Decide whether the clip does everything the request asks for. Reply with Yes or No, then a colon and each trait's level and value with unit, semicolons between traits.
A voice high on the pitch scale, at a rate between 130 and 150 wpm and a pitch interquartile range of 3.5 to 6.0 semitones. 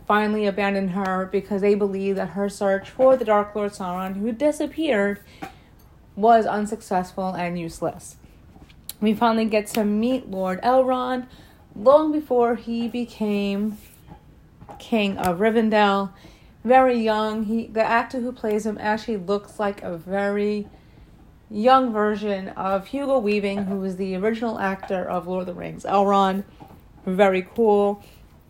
No: high, 205 Hz; slow, 135 wpm; average, 2.7 semitones